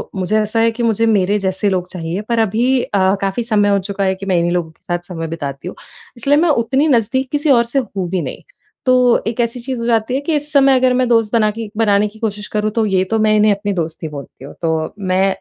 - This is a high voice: Yes, high, 210 Hz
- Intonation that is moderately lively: Yes, average, 3.9 semitones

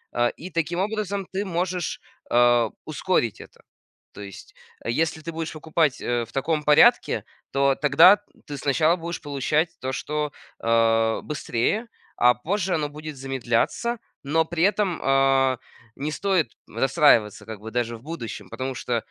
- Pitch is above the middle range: No, medium, 145 Hz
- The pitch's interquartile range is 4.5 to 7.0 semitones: Yes, wide, 5.4 semitones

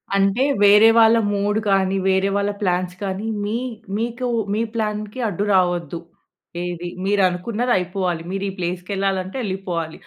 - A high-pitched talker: Yes, high, 195 Hz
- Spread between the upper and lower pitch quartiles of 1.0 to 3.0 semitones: Yes, narrow, 2.5 semitones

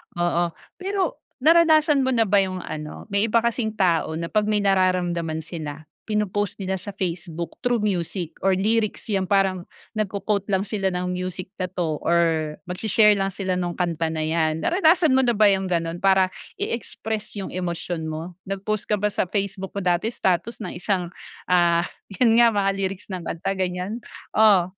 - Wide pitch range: No, average, 3.4 semitones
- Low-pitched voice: No, high, 190 Hz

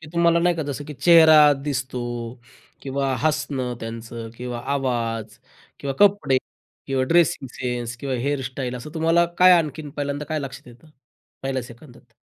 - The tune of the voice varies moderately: Yes, average, 4.2 semitones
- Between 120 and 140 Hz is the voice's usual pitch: Yes, low, 135 Hz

